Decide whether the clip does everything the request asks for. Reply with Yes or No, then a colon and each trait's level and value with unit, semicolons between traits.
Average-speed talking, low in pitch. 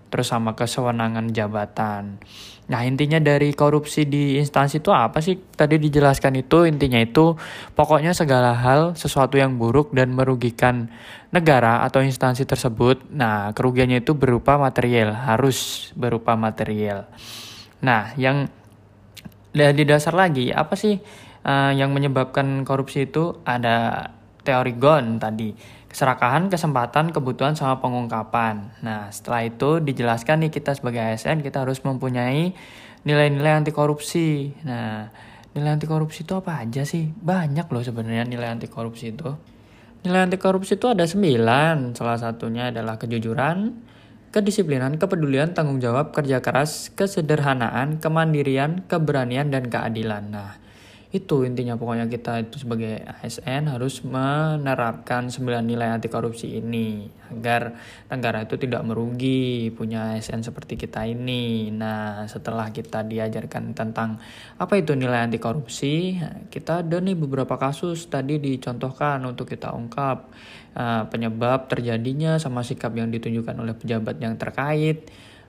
Yes: average, 130 wpm; low, 130 Hz